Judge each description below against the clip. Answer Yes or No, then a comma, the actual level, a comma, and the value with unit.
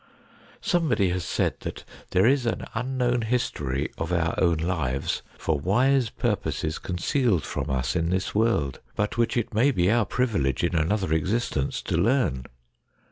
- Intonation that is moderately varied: No, wide, 6.8 semitones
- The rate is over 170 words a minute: No, average, 160 wpm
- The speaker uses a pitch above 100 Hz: No, very low, 95 Hz